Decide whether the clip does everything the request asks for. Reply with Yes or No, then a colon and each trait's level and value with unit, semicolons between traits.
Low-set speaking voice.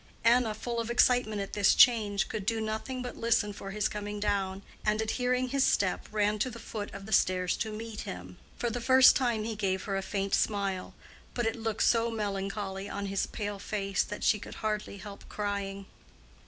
No: high, 210 Hz